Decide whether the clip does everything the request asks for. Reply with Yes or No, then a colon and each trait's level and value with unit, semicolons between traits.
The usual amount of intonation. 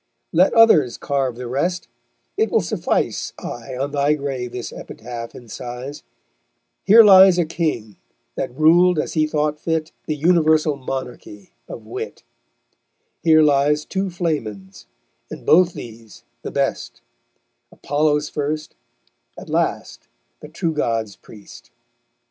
Yes: average, 4.7 semitones